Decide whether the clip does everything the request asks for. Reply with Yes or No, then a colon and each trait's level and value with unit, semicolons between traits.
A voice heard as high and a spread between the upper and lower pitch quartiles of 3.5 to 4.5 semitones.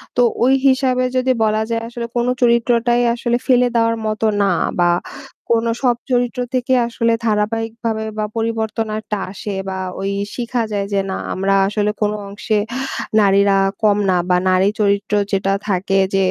No: high, 220 Hz; average, 2.9 semitones